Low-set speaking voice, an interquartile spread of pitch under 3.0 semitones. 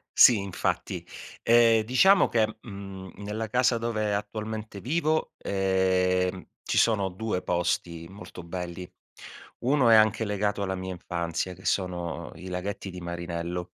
No: low, 100 Hz; average, 3.4 semitones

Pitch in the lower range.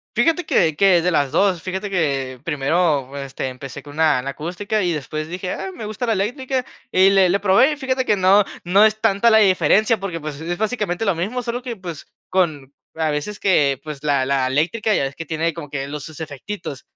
No: medium, 175 Hz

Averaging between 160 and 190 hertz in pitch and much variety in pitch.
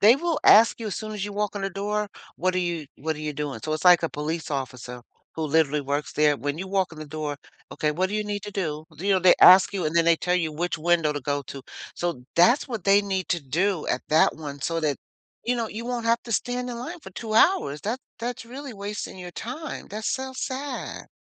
Yes: medium, 185 Hz; wide, 5.9 semitones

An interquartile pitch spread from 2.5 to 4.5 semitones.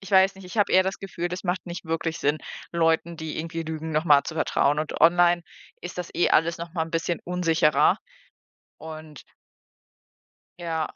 No: narrow, 1.8 semitones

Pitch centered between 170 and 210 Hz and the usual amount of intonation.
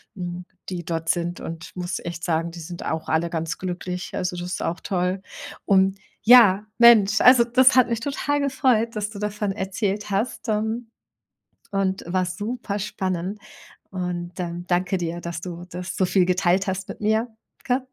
Yes: high, 190 Hz; average, 3.4 semitones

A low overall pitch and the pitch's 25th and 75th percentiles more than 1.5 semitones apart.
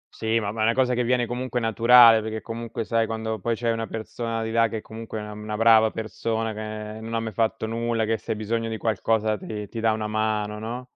No: low, 110 Hz; narrow, 1.0 semitones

